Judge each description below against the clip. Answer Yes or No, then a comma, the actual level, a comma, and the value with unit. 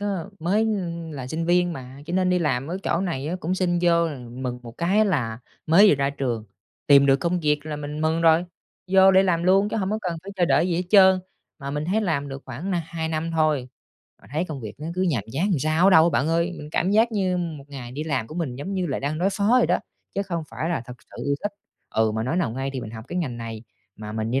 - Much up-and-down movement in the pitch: No, average, 4.9 semitones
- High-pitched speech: No, medium, 160 Hz